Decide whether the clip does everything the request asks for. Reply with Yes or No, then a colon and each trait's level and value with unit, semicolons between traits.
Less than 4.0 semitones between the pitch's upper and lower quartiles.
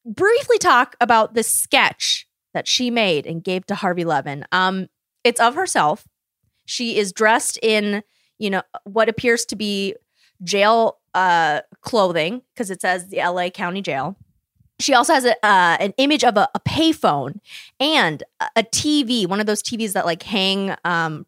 No: average, 4.5 semitones